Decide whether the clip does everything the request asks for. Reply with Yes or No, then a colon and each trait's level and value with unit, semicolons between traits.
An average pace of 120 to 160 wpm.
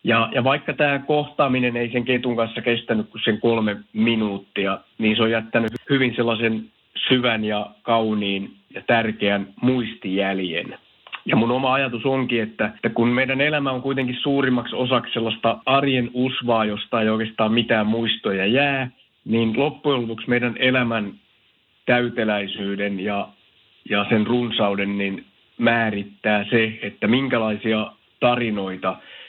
Yes: average, 135 wpm